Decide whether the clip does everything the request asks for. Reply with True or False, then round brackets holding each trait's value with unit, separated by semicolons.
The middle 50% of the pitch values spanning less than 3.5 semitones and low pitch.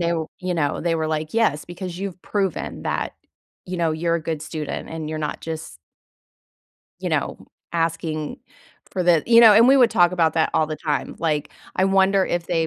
False (2.8 semitones; 170 Hz)